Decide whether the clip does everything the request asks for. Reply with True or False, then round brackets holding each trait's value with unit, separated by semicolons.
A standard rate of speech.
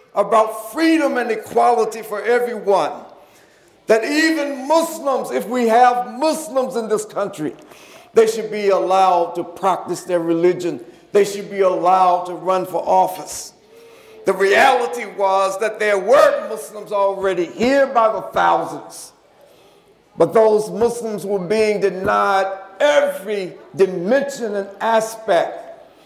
False (125 wpm)